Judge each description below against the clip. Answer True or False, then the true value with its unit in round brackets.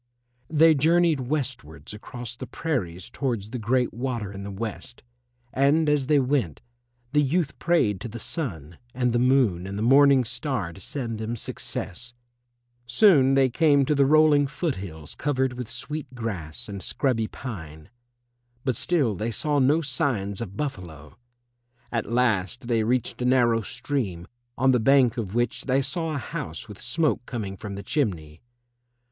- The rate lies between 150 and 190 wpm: True (165 wpm)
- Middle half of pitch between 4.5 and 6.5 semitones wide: True (5.2 semitones)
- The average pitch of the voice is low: True (125 Hz)